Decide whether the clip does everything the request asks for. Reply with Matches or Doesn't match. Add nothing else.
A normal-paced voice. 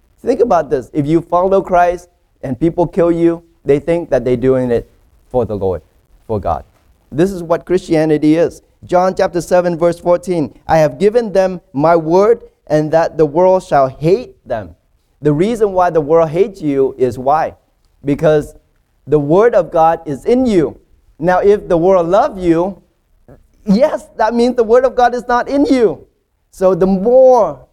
Matches